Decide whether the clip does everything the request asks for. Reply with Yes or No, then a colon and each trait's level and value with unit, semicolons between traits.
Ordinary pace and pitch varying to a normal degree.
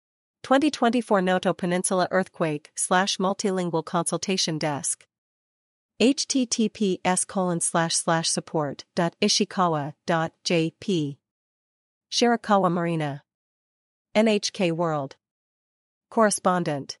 No: slow, 80 wpm; average, 3.9 semitones